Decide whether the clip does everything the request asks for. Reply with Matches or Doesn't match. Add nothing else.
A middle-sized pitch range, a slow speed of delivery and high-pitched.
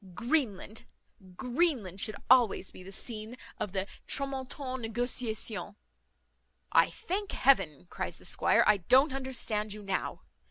Matches